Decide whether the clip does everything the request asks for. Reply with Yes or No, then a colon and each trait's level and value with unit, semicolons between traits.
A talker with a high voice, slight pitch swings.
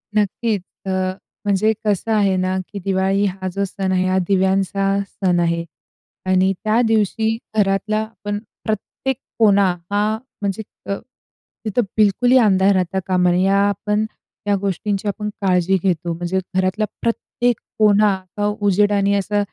Yes: high, 200 Hz; narrow, 1.9 semitones